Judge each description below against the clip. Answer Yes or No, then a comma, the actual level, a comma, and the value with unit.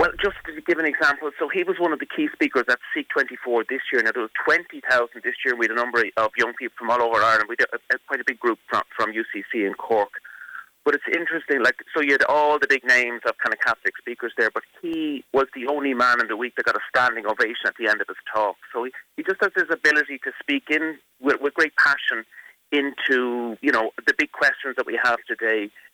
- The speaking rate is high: Yes, fast, 255 wpm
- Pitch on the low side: No, medium, 145 Hz